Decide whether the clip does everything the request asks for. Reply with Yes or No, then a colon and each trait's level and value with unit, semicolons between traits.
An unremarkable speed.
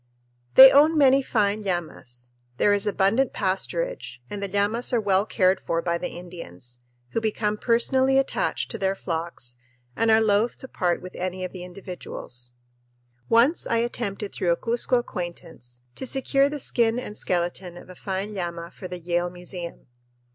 Yes: average, 170 wpm